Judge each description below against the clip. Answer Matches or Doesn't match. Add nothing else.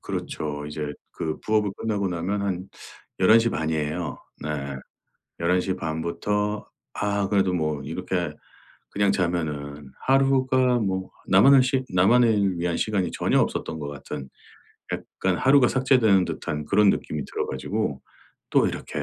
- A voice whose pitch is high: Doesn't match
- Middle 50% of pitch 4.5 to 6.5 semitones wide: Matches